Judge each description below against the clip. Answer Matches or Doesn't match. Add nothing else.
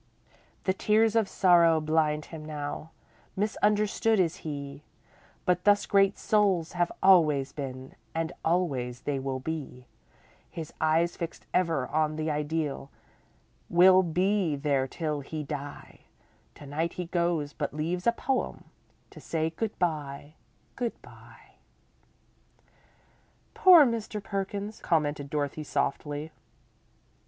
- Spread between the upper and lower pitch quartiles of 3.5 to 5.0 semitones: Matches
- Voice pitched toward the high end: Doesn't match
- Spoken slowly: Matches